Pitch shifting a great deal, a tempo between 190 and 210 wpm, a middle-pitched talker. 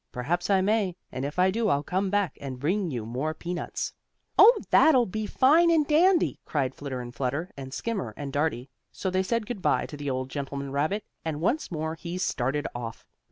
Yes: wide, 6.8 semitones; fast, 205 wpm; medium, 165 Hz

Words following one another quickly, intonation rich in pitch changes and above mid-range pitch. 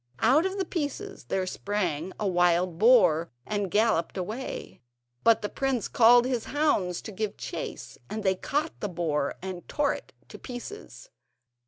No: average, 160 wpm; wide, 6.4 semitones; high, 215 Hz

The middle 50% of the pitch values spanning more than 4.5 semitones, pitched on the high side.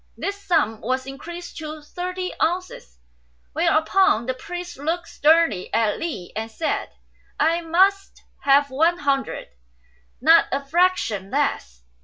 Yes: average, 5.2 semitones; very high, 315 Hz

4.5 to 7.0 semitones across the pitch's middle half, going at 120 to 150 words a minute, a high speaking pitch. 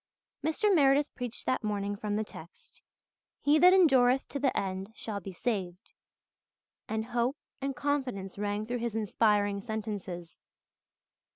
Yes: average, 4.9 semitones; slow, 135 wpm; high, 220 Hz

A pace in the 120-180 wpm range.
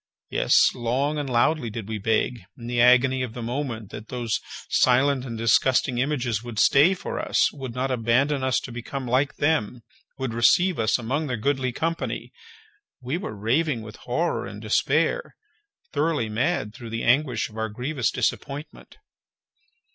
Yes: average, 160 wpm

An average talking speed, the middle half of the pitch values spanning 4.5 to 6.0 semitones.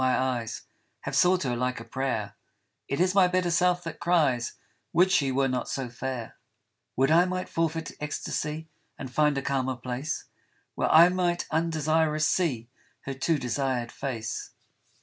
Yes: average, 170 wpm; average, 4.8 semitones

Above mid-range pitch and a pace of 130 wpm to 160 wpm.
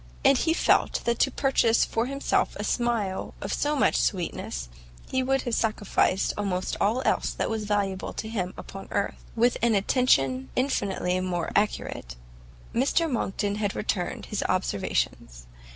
Yes: high, 210 Hz; average, 150 wpm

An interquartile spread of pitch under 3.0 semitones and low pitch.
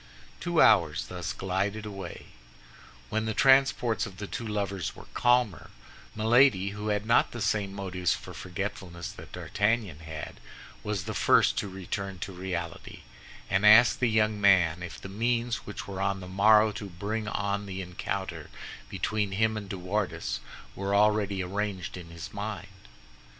Yes: narrow, 2.5 semitones; low, 100 Hz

